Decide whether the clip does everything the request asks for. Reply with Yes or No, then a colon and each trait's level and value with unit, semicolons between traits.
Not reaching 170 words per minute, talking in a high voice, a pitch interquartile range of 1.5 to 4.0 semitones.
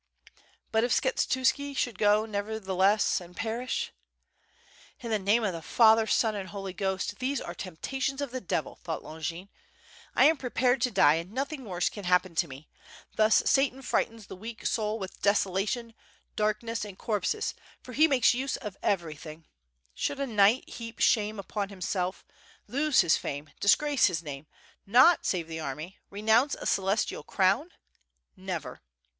No: average, 160 wpm; high, 210 Hz; average, 4.9 semitones